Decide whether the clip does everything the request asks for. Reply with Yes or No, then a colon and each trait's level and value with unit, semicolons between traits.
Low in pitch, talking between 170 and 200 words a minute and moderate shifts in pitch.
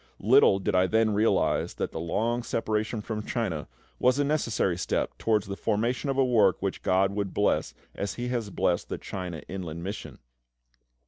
Yes: low, 105 Hz; average, 180 wpm; average, 3.7 semitones